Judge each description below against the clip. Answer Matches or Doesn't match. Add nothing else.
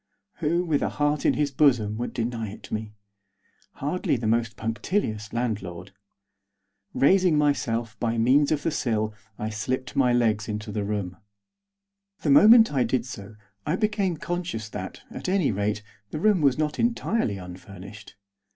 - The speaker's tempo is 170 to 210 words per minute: Doesn't match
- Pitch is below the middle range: Matches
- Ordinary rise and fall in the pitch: Doesn't match